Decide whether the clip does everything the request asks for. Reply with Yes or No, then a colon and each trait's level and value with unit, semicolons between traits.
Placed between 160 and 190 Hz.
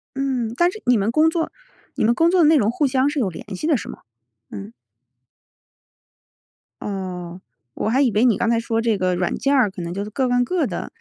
No: high, 235 Hz